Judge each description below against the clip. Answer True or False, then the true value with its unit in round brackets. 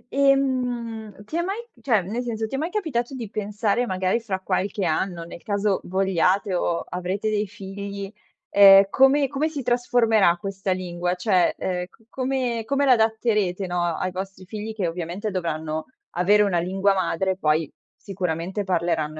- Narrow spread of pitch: False (4.2 semitones)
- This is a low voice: False (200 Hz)